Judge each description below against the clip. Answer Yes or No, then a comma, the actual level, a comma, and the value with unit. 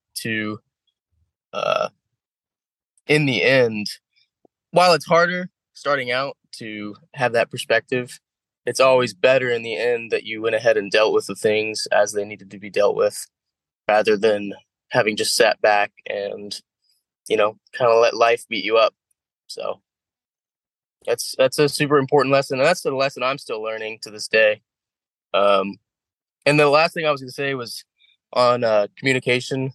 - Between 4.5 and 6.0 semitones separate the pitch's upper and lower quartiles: Yes, average, 5.3 semitones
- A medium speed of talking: Yes, average, 165 wpm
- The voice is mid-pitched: No, low, 125 Hz